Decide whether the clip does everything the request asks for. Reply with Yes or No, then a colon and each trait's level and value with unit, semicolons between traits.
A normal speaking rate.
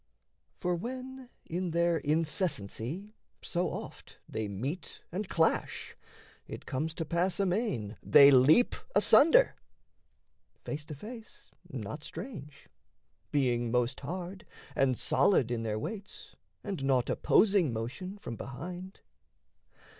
No: slow, 115 wpm